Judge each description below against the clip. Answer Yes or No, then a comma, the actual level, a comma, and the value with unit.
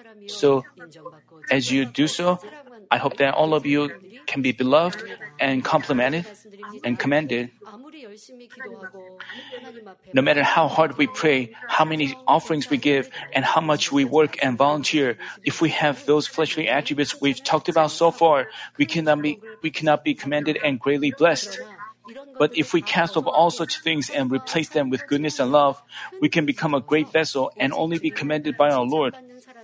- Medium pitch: Yes, medium, 155 Hz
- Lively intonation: No, average, 3.6 semitones